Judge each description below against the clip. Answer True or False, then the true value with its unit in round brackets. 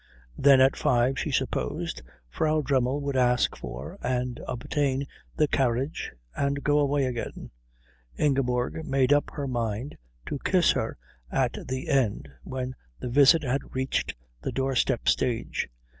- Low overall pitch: True (130 Hz)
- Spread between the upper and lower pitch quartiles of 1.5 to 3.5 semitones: True (2.4 semitones)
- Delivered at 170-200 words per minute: False (140 wpm)